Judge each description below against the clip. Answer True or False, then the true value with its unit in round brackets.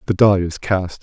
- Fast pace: True (235 wpm)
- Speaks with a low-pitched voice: True (95 Hz)